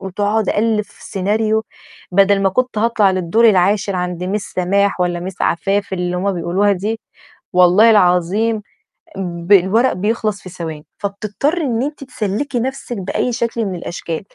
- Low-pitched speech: No, high, 200 Hz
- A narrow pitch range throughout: No, average, 3.5 semitones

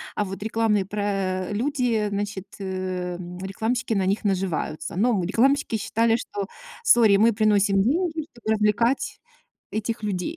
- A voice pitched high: Yes, high, 210 Hz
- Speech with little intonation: No, average, 3.0 semitones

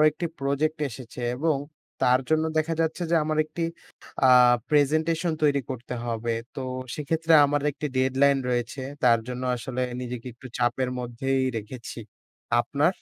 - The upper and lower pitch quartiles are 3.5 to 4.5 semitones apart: Yes, average, 3.9 semitones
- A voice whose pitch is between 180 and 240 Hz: No, low, 135 Hz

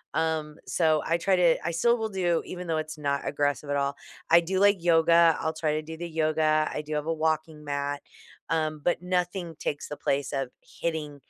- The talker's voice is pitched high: No, medium, 160 Hz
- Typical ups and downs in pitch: No, narrow, 2.1 semitones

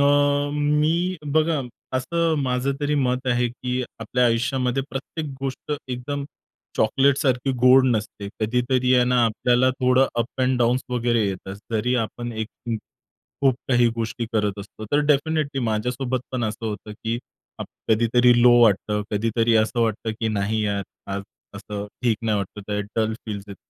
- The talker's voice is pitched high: No, low, 125 Hz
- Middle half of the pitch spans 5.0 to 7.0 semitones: No, average, 3.3 semitones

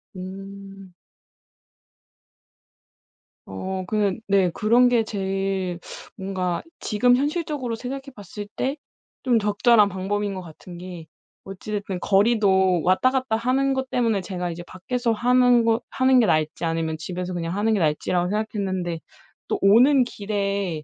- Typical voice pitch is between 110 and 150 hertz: No, high, 200 Hz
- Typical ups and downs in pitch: Yes, average, 4.2 semitones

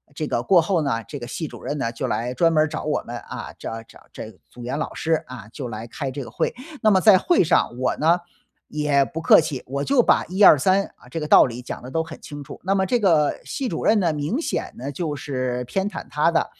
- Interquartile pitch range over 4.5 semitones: Yes, wide, 5.4 semitones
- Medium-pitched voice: Yes, medium, 150 Hz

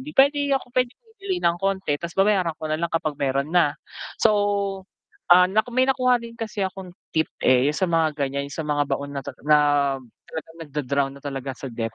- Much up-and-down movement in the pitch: Yes, wide, 6.8 semitones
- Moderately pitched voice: Yes, medium, 160 Hz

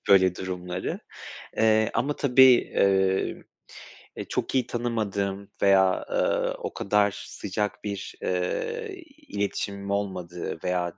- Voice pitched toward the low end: Yes, low, 100 Hz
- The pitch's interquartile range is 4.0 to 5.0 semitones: No, average, 2.9 semitones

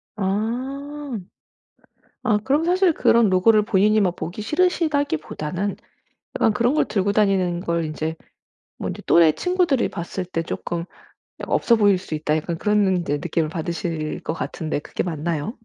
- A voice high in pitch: Yes, high, 195 Hz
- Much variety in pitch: Yes, wide, 5.9 semitones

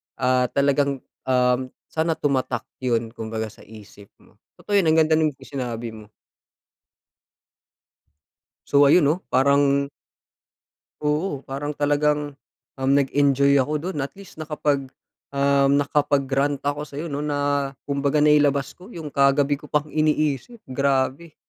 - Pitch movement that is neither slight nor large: No, narrow, 1.8 semitones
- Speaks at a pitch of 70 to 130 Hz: No, medium, 140 Hz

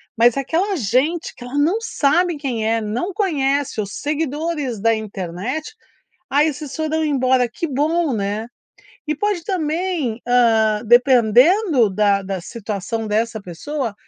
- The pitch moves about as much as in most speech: No, wide, 6.1 semitones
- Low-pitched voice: No, very high, 260 Hz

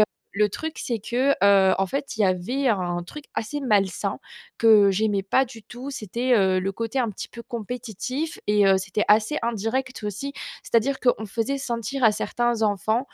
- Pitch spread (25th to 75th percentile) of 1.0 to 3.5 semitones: No, average, 4.1 semitones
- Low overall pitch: No, high, 225 Hz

